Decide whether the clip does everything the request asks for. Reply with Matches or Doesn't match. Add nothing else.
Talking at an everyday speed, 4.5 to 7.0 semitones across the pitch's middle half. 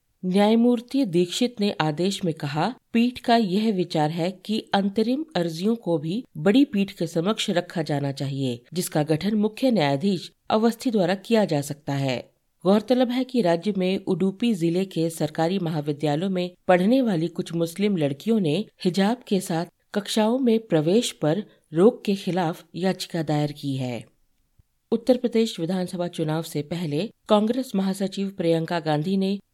Matches